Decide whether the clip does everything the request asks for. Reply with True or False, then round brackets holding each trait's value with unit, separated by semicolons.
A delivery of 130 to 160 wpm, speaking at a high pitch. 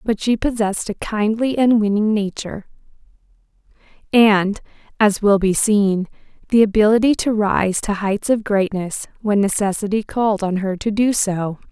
True (150 wpm; 210 Hz)